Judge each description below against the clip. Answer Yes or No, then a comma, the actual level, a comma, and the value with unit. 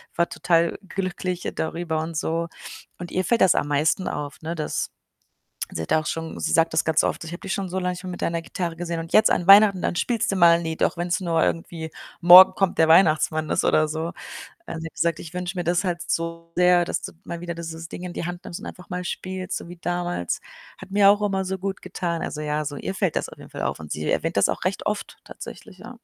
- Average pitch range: No, narrow, 1.9 semitones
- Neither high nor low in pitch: Yes, medium, 170 Hz